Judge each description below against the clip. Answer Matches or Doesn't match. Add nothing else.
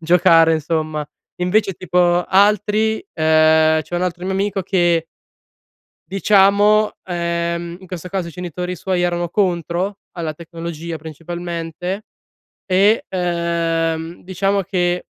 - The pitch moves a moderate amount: Doesn't match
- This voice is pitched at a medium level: Matches